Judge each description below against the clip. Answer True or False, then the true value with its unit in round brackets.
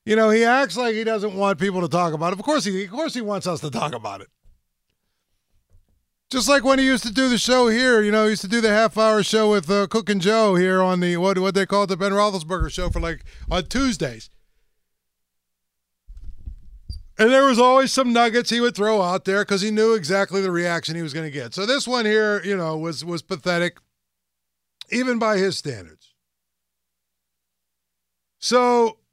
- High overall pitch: True (195 Hz)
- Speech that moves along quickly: True (210 wpm)